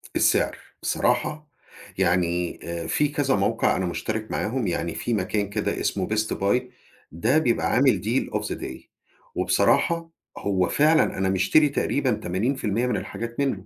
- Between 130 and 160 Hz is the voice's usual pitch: No, low, 110 Hz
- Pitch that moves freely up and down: Yes, wide, 5.9 semitones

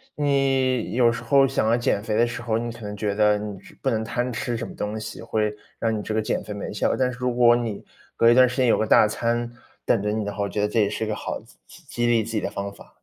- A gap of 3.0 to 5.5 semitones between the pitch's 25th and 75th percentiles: No, narrow, 2.4 semitones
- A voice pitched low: Yes, low, 115 Hz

